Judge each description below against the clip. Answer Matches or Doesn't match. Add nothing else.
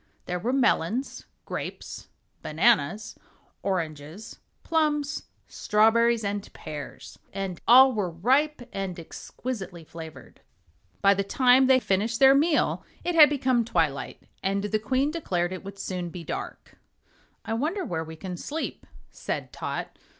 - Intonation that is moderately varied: Doesn't match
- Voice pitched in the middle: Doesn't match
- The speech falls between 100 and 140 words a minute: Matches